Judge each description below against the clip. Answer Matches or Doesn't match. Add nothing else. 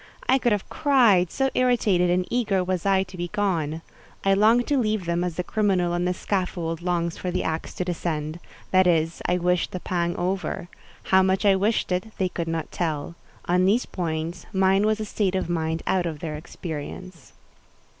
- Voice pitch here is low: Doesn't match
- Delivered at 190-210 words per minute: Matches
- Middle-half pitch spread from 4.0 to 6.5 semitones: Doesn't match